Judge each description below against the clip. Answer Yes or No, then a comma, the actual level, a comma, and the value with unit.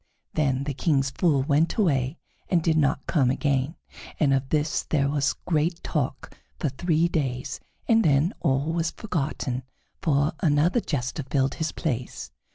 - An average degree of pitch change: Yes, average, 3.3 semitones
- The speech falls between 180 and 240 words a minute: No, average, 155 wpm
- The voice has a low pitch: No, medium, 145 Hz